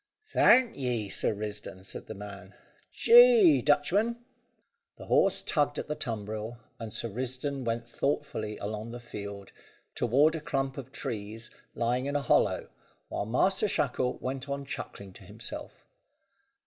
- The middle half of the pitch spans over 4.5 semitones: Yes, average, 5.2 semitones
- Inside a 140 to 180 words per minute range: Yes, average, 145 wpm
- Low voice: Yes, low, 125 Hz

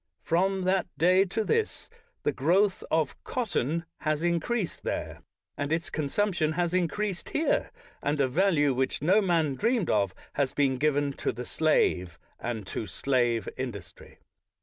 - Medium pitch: Yes, medium, 160 Hz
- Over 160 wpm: No, average, 150 wpm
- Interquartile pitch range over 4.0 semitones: Yes, wide, 5.6 semitones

